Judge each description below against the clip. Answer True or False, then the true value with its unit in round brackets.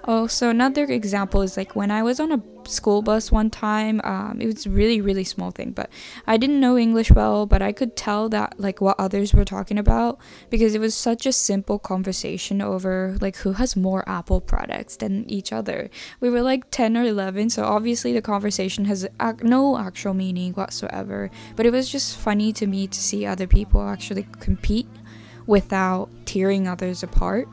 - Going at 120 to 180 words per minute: False (190 wpm)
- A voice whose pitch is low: False (205 Hz)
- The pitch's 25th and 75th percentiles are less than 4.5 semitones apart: True (3.2 semitones)